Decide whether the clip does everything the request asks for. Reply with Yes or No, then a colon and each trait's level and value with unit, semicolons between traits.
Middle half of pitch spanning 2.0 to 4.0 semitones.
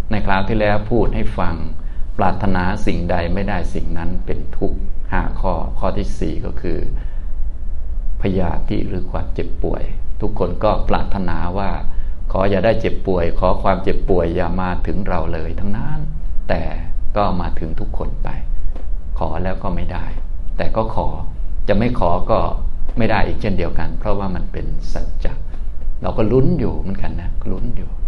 No: average, 4.8 semitones